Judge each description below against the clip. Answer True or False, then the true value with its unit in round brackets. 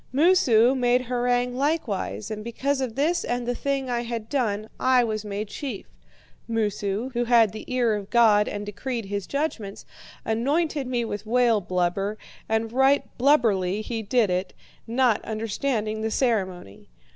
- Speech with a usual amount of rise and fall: True (3.4 semitones)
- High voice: True (230 Hz)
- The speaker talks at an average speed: True (155 wpm)